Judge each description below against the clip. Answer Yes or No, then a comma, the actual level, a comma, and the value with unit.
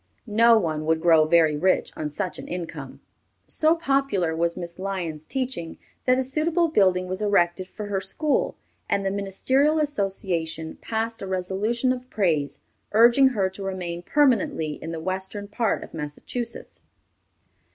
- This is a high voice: Yes, high, 195 Hz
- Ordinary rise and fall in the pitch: No, wide, 5.8 semitones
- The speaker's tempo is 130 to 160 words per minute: Yes, average, 150 wpm